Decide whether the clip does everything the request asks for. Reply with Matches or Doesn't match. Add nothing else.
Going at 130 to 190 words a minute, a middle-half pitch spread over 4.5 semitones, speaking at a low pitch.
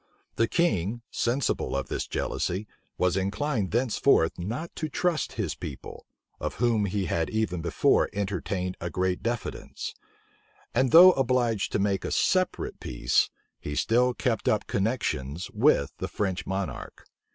Matches